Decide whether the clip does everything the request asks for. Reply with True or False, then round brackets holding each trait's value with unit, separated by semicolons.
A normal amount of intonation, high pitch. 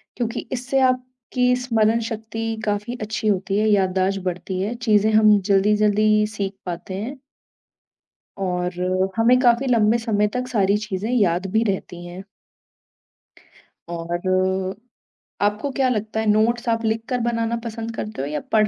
True (3.3 semitones; 215 Hz)